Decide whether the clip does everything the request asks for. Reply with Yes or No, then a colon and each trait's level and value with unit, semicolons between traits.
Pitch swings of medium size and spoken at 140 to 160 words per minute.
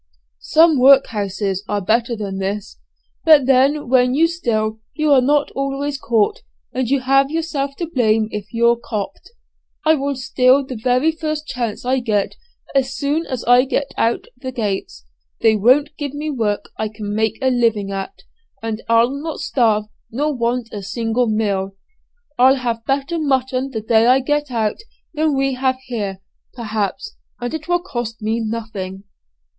No: average, 4.1 semitones; average, 170 wpm